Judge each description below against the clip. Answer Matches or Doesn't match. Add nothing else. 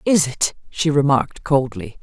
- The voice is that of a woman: Matches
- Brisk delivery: Doesn't match